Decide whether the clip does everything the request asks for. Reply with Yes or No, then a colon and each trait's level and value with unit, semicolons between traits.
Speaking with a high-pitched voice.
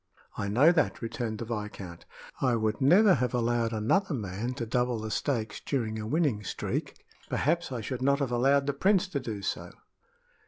No: low, 120 Hz